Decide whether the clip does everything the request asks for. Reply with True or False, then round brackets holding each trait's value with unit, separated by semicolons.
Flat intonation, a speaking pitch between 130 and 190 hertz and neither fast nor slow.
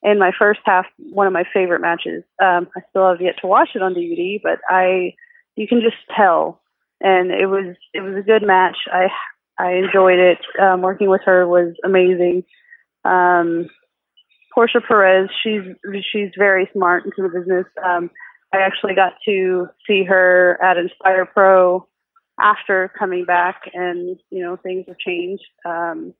True (1.6 semitones; 185 Hz; 165 wpm)